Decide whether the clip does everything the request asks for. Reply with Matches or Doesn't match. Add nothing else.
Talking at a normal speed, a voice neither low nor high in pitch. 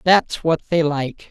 Matches